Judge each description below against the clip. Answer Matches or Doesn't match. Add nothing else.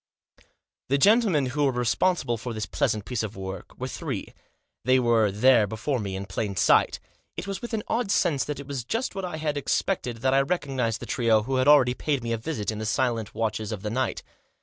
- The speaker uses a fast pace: Matches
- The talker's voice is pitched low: Matches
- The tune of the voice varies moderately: Matches